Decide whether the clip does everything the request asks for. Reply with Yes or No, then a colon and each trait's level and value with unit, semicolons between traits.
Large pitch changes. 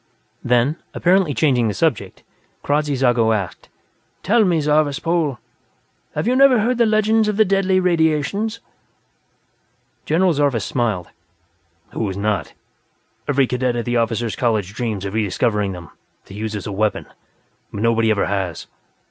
Yes: wide, 8.2 semitones